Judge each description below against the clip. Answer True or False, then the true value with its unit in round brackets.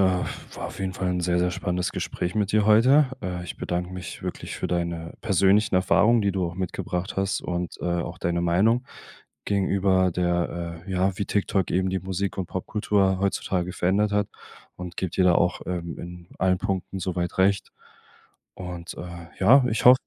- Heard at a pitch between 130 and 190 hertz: False (95 Hz)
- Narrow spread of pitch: True (2.0 semitones)